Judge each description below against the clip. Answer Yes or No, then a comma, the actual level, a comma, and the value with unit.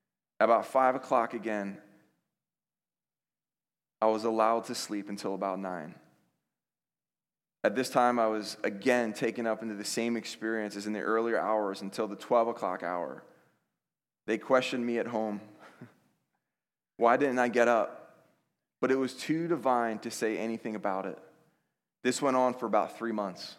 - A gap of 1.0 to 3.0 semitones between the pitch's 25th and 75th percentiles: Yes, narrow, 2.6 semitones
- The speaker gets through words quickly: No, average, 155 wpm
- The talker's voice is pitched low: Yes, low, 115 Hz